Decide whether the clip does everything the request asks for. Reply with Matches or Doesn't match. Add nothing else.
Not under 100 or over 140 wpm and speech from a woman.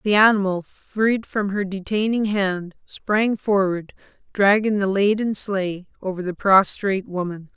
Matches